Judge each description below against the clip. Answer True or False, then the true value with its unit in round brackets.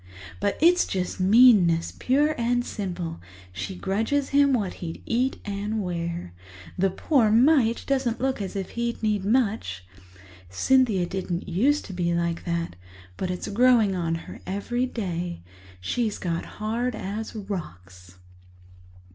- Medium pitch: False (200 Hz)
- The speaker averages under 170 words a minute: True (140 wpm)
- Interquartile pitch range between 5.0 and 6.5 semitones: True (5.6 semitones)